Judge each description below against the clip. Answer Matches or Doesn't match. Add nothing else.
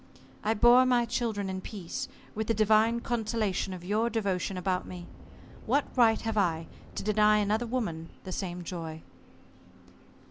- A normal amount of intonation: Matches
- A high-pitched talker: Matches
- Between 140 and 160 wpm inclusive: Matches